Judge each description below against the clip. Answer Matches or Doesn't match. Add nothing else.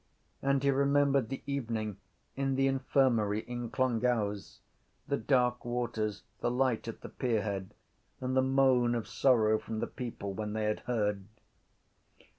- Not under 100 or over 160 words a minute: Matches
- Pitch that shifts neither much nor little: Matches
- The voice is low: Matches